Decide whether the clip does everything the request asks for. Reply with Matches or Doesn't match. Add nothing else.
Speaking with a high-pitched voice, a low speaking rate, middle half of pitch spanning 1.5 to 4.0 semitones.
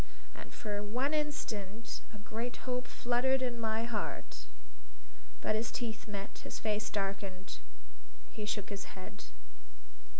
Matches